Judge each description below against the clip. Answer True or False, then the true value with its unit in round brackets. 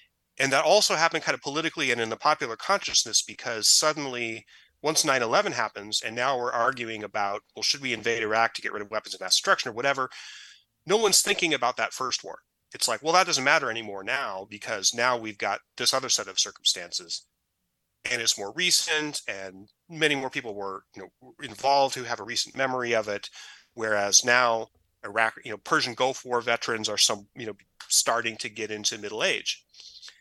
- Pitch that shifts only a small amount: False (4.5 semitones)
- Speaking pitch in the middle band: False (120 Hz)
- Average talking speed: True (195 wpm)